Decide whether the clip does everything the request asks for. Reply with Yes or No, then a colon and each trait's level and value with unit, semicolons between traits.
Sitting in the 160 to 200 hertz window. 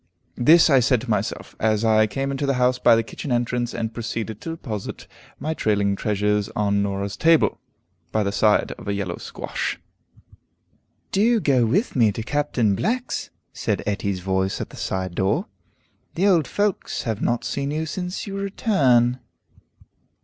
No: low, 120 Hz